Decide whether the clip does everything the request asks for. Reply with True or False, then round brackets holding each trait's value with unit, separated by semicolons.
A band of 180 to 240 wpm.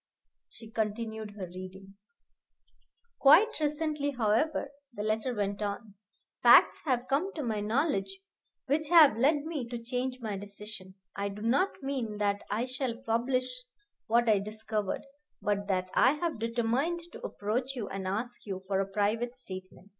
False (155 wpm)